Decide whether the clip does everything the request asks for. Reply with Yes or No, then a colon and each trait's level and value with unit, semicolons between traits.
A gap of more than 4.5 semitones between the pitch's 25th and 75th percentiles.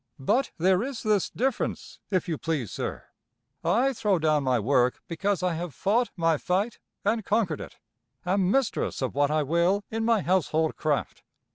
Yes: wide, 5.5 semitones